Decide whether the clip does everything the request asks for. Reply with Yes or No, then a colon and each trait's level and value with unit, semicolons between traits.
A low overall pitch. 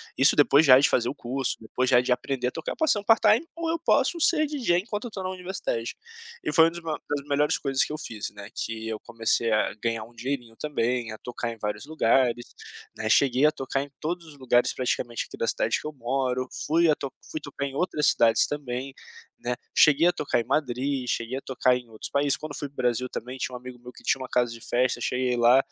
Yes: low, 130 Hz